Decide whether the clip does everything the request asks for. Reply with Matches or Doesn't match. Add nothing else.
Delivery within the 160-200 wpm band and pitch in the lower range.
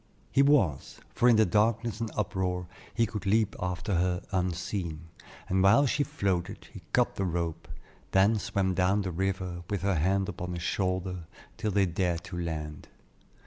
Matches